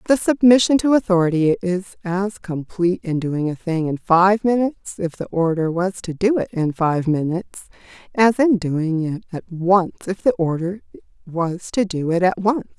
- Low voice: No, medium, 185 Hz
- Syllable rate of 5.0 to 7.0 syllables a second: No, 4.8 syllables/s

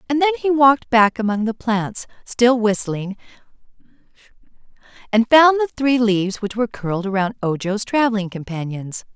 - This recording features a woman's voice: Yes, female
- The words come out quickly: No, average, 145 wpm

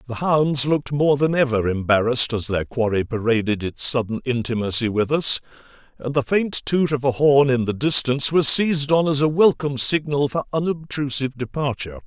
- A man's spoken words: Yes, male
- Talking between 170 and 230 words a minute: Yes, average, 180 wpm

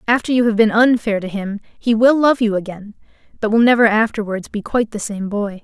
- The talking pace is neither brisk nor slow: No, fast, 225 wpm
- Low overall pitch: No, high, 220 Hz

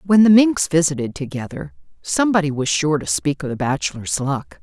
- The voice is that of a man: No, female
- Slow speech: No, average, 180 wpm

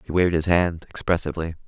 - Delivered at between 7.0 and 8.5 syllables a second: Yes, 7.1 syllables/s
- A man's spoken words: Yes, male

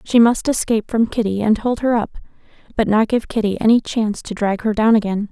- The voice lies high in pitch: Yes, high, 220 Hz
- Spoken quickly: Yes, fast, 225 wpm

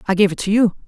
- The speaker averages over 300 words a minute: Yes, fast, 345 wpm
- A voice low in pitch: No, high, 200 Hz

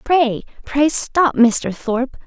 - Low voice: No, very high, 260 Hz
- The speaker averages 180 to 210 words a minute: No, slow, 135 wpm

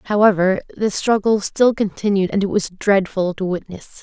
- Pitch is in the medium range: No, high, 200 Hz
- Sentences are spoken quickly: No, average, 165 wpm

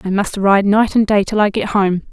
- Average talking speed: No, fast, 285 wpm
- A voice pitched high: Yes, high, 200 Hz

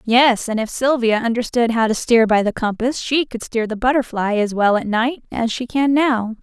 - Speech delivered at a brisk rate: Yes, fast, 225 wpm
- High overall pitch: Yes, high, 235 Hz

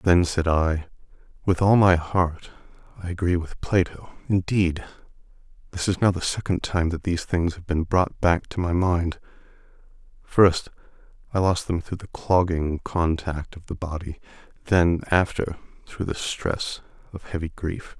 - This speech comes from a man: Yes, male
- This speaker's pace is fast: No, average, 155 wpm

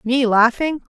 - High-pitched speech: Yes, very high, 250 Hz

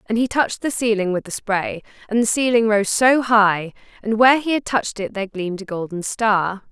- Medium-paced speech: No, fast, 225 wpm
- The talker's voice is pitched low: No, high, 215 Hz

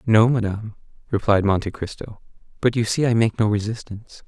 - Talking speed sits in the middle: Yes, average, 170 wpm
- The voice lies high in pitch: No, low, 110 Hz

